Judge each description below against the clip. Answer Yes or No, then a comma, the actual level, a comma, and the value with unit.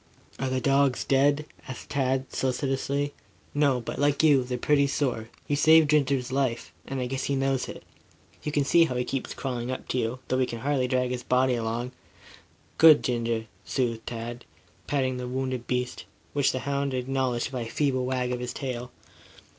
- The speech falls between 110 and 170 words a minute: No, average, 185 wpm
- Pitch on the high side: No, low, 130 Hz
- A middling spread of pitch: No, narrow, 2.0 semitones